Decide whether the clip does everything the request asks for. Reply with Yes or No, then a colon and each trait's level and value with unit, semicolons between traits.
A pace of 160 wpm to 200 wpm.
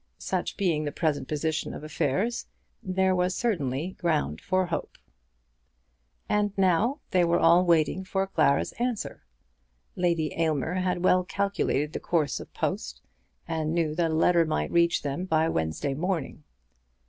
No: average, 150 wpm